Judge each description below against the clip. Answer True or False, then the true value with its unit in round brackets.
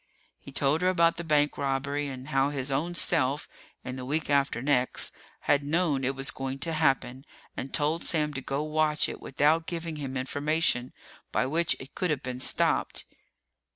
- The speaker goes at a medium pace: True (185 wpm)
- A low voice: False (145 Hz)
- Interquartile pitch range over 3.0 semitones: False (2.7 semitones)